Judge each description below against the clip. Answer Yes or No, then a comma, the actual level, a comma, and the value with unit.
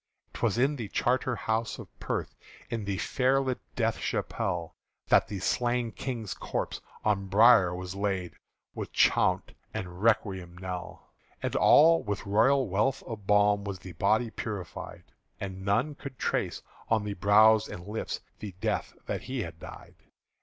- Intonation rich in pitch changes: No, average, 3.9 semitones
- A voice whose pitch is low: Yes, low, 105 Hz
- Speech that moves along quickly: No, average, 155 wpm